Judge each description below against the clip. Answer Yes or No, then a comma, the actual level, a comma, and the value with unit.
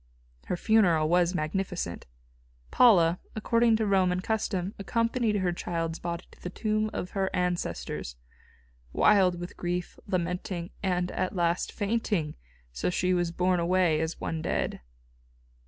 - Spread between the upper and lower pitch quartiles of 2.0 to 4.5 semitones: Yes, narrow, 2.6 semitones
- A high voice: No, medium, 180 Hz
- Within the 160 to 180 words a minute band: No, average, 140 wpm